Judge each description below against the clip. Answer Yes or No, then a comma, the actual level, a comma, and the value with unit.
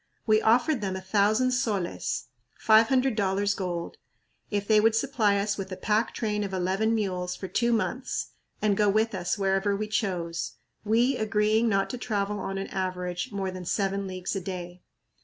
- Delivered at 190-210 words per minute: No, average, 180 wpm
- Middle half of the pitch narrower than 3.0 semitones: Yes, narrow, 2.5 semitones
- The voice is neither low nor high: No, high, 205 Hz